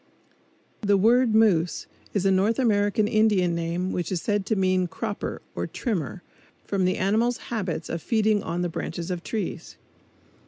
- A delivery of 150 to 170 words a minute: Yes, average, 160 wpm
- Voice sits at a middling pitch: No, high, 195 Hz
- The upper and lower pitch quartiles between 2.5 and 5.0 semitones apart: Yes, average, 3.4 semitones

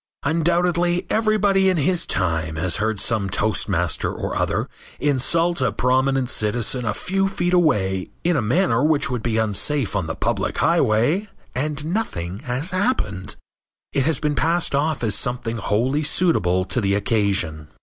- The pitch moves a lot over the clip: Yes, wide, 8.3 semitones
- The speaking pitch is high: No, low, 130 Hz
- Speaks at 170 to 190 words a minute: No, average, 155 wpm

